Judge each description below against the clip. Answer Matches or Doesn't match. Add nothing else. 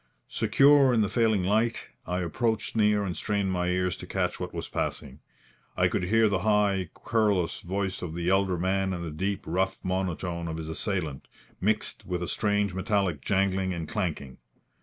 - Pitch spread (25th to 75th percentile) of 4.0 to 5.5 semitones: Doesn't match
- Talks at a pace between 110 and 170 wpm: Doesn't match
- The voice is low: Matches